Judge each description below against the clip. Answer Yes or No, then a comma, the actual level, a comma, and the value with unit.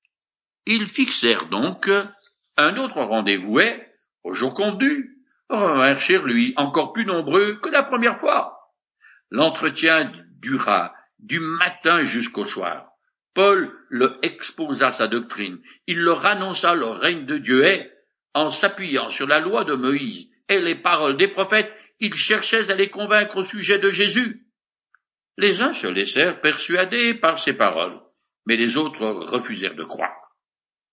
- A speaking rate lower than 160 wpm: Yes, slow, 145 wpm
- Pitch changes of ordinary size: No, wide, 6.0 semitones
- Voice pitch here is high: Yes, high, 200 Hz